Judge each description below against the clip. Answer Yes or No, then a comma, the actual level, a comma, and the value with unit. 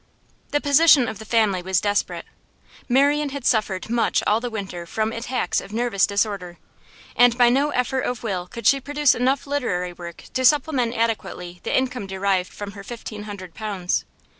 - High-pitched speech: Yes, high, 225 Hz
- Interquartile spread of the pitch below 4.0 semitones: No, average, 4.5 semitones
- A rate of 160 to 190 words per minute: Yes, average, 175 wpm